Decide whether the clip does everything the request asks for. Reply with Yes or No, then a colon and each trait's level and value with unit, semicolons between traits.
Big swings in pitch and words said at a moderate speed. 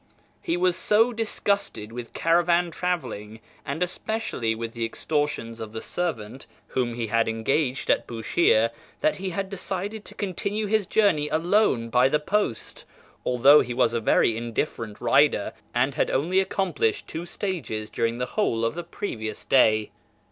Yes: wide, 8.0 semitones; average, 155 wpm